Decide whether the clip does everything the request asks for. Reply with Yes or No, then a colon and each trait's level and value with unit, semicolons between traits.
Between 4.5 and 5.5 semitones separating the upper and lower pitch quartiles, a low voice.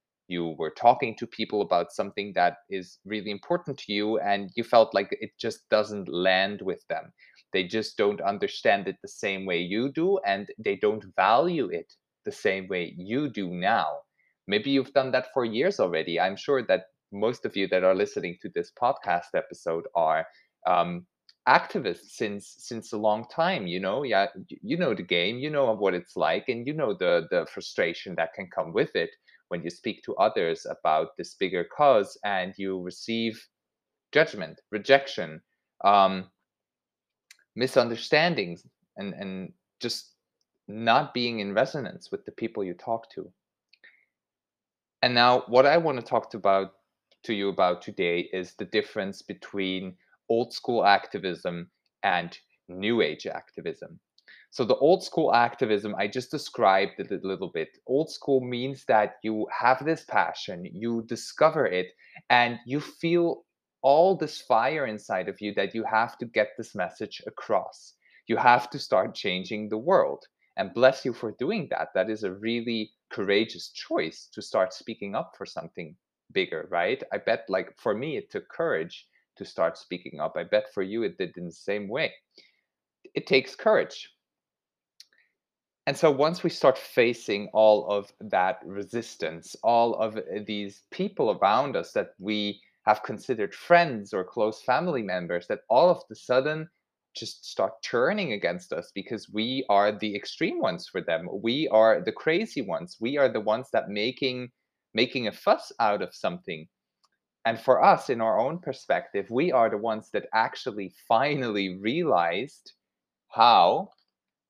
Yes: average, 4.8 semitones; low, 110 Hz